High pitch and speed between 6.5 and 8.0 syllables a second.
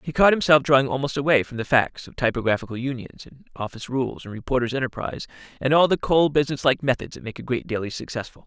No: low, 130 Hz; 6.8 syllables/s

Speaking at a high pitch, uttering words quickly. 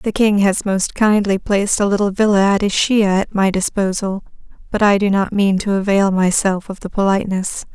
No: high, 200 Hz; average, 195 wpm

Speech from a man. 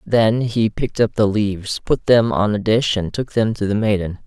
Yes: male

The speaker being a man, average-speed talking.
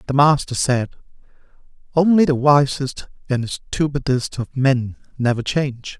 No: male; slow, 120 wpm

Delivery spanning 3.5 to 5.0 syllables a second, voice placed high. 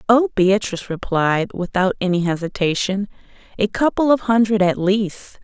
Yes: 4.8 syllables/s; high, 200 Hz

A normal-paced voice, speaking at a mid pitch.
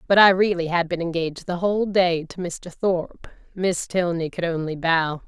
Yes: average, 195 wpm; medium, 175 Hz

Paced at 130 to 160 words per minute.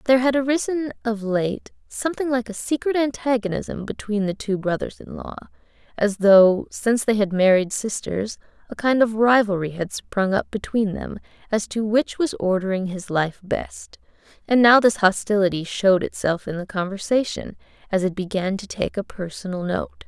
No: average, 170 wpm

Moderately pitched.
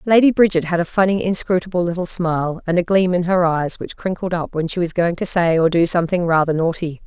Yes: medium, 175 Hz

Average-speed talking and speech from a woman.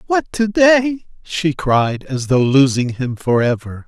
No: average, 170 wpm; male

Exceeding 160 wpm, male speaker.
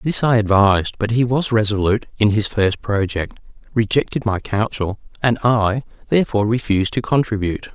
No: average, 155 wpm; male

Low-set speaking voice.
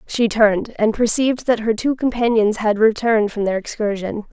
No: high, 220 Hz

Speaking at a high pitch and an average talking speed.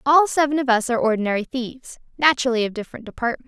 Yes: very high, 250 Hz; average, 175 wpm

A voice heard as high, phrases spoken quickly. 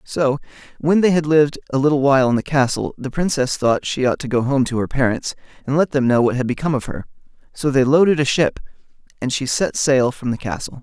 No: low, 135 Hz; fast, 240 wpm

